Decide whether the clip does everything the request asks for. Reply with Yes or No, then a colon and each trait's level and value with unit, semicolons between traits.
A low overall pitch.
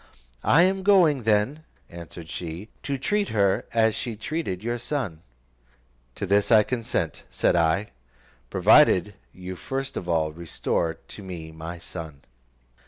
Yes: low, 100 Hz